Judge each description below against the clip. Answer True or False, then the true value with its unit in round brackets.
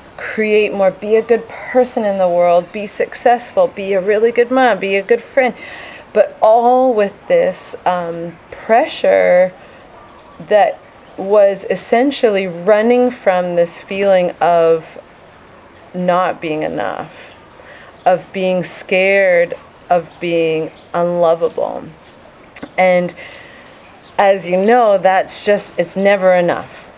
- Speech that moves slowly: True (115 wpm)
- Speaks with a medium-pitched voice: False (195 Hz)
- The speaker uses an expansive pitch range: False (4.8 semitones)